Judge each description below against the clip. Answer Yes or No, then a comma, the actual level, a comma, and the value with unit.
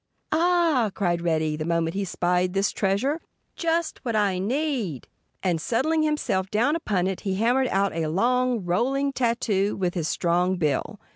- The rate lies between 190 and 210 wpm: No, average, 160 wpm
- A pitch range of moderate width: No, wide, 6.7 semitones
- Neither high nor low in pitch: No, high, 200 Hz